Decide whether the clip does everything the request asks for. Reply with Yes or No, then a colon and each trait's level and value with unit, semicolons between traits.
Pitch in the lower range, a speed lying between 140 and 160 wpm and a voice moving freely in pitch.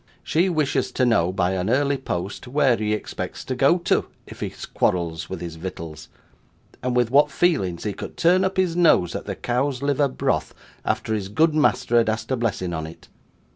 No: low, 120 Hz; average, 200 wpm; wide, 7.7 semitones